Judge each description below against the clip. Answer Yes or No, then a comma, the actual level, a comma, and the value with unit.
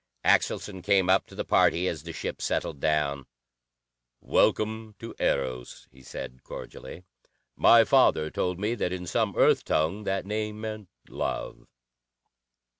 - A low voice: Yes, very low, 90 Hz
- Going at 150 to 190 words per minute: No, average, 140 wpm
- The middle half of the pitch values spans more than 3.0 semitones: Yes, wide, 5.5 semitones